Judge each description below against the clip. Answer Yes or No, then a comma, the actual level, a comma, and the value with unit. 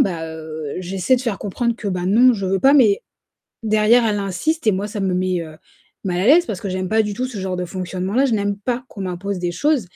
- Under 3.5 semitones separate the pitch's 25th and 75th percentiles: No, average, 4.0 semitones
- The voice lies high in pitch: Yes, high, 200 Hz